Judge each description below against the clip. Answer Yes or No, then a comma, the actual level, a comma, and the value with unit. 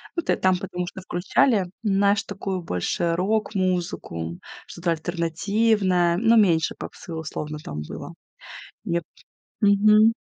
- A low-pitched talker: No, medium, 185 Hz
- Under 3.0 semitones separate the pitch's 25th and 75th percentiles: No, average, 3.3 semitones